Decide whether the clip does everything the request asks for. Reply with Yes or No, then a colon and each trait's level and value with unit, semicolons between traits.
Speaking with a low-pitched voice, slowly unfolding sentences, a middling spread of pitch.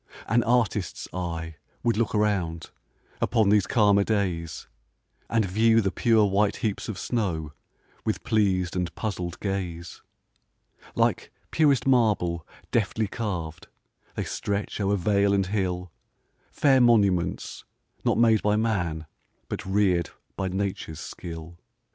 Yes: low, 100 Hz; slow, 125 wpm; average, 3.7 semitones